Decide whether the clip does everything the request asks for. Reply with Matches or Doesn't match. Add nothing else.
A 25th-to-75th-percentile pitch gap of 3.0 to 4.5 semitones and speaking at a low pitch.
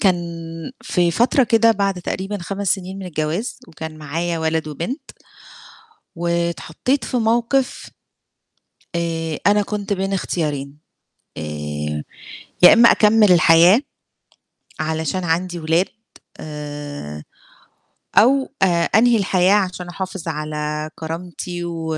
Doesn't match